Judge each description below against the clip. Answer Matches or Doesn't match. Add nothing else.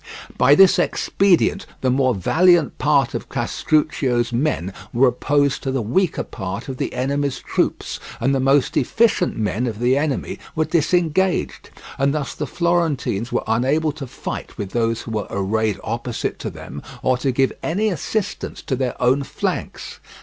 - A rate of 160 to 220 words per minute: Matches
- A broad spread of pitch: Doesn't match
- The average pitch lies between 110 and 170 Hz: Matches